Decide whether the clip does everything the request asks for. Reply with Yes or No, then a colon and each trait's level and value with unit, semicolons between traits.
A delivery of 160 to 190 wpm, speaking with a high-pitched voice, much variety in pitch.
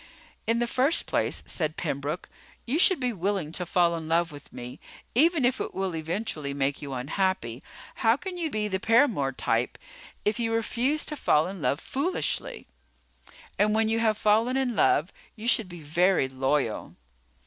Yes: average, 175 wpm; high, 195 Hz; wide, 7.6 semitones